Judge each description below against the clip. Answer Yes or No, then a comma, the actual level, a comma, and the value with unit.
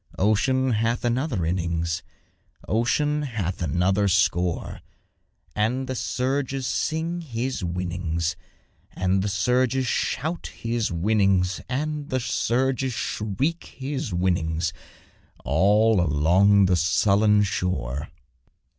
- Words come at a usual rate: No, slow, 100 wpm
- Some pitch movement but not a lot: No, wide, 6.3 semitones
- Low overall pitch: Yes, low, 105 Hz